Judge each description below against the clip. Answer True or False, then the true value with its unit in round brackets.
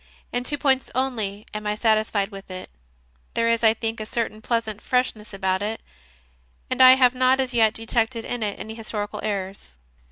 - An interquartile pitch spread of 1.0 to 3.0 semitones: True (2.6 semitones)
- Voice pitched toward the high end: True (225 Hz)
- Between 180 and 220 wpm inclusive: True (185 wpm)